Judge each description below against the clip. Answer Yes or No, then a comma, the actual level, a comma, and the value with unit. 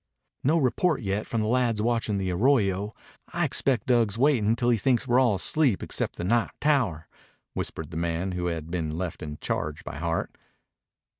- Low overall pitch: Yes, low, 105 Hz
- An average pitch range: No, wide, 5.9 semitones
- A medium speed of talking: Yes, average, 180 wpm